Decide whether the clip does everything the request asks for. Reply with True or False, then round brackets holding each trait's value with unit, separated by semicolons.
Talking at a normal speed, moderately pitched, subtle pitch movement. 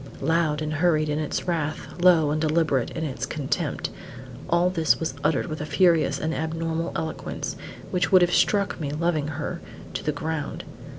True (175 wpm; 160 Hz; 2.0 semitones)